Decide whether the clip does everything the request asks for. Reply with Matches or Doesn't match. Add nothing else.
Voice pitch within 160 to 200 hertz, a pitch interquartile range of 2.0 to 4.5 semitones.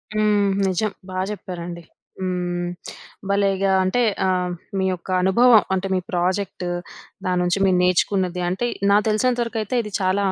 Matches